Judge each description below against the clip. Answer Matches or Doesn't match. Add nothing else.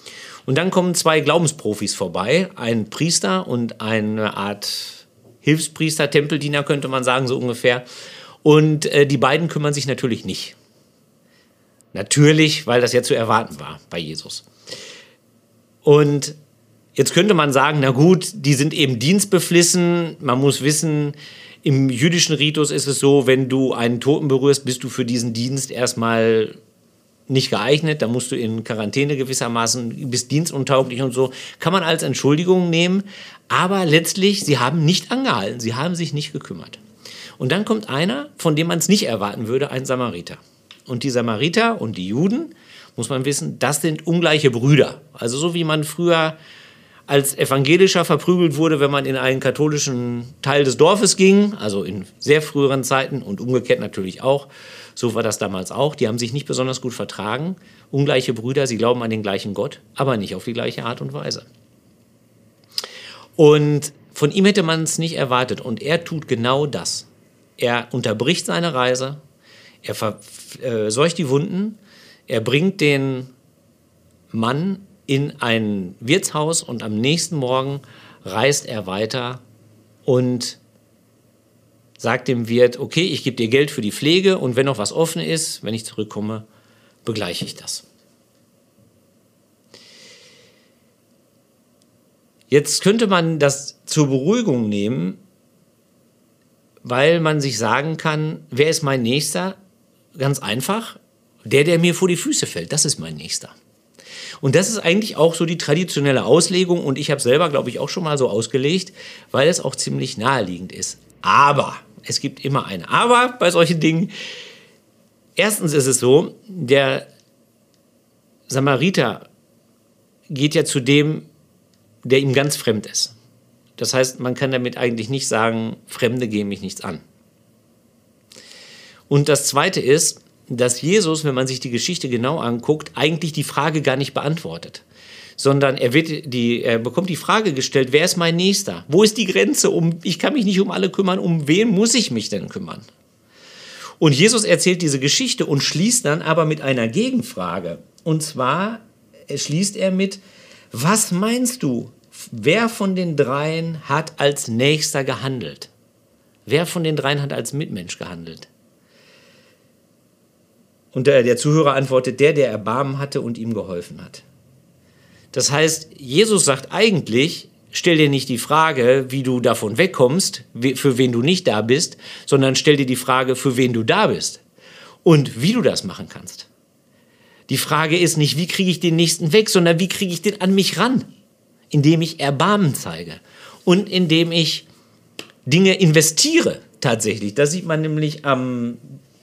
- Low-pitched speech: Doesn't match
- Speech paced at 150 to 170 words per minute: Matches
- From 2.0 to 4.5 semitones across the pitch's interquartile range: Doesn't match